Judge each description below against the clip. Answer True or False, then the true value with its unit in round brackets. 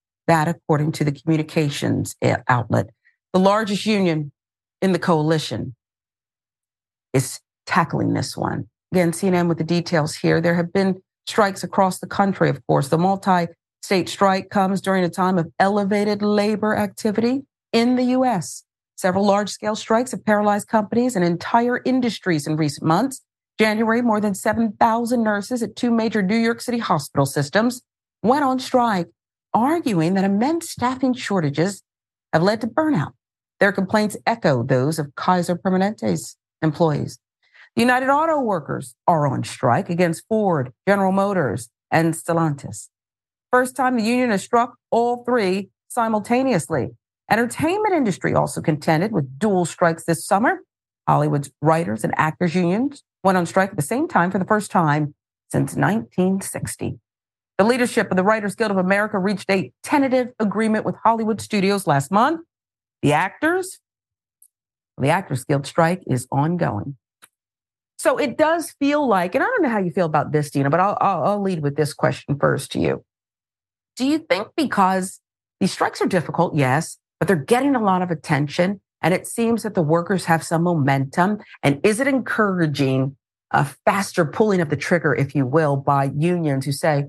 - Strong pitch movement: True (6.1 semitones)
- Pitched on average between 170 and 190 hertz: True (185 Hz)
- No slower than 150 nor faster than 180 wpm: True (160 wpm)